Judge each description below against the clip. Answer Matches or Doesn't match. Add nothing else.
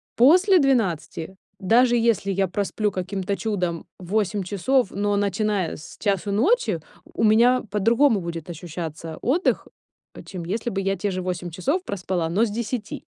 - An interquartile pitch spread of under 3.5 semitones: Doesn't match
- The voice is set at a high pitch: Matches